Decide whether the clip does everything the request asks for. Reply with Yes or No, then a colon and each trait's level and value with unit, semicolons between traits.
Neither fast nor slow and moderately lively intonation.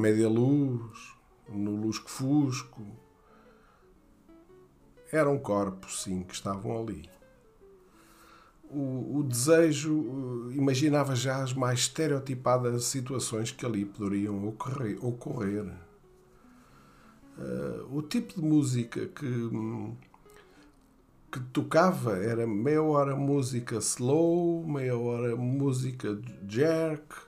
No: slow, 90 wpm; average, 4.6 semitones